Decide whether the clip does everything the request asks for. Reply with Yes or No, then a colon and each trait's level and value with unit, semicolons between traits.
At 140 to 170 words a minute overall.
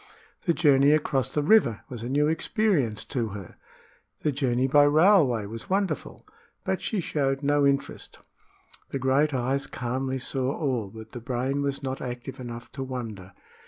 Yes: average, 160 wpm